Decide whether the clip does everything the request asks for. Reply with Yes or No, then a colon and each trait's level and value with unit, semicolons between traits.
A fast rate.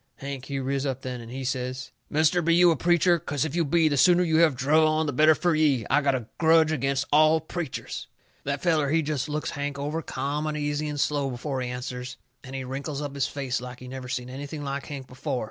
Yes: fast, 245 wpm